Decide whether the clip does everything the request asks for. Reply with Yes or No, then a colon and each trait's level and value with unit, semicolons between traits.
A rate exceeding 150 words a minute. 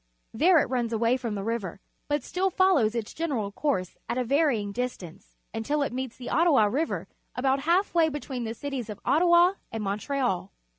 Yes: average, 185 wpm